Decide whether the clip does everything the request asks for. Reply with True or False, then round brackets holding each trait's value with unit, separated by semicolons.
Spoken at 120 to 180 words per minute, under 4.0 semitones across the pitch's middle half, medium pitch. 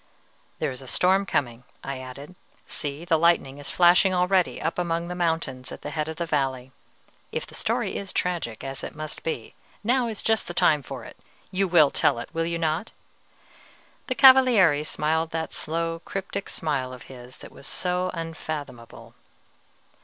False (175 wpm; 4.5 semitones; 165 Hz)